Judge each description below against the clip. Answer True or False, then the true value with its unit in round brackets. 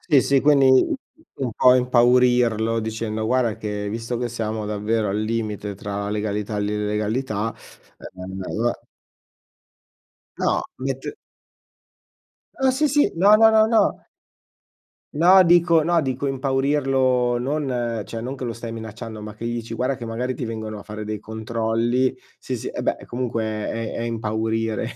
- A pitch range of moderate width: True (3.3 semitones)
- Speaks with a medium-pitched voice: False (115 Hz)